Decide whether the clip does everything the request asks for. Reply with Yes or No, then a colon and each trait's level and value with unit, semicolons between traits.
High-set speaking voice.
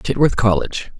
No: low, 115 Hz